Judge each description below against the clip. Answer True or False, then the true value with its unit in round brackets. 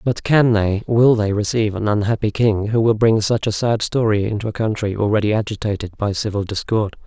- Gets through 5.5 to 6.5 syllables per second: True (5.6 syllables/s)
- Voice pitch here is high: False (110 Hz)